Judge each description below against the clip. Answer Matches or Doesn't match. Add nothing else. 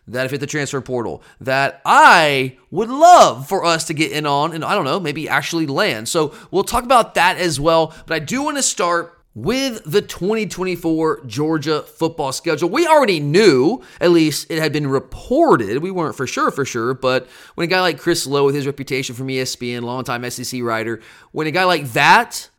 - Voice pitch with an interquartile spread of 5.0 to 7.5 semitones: Matches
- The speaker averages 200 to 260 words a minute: Matches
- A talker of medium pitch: Matches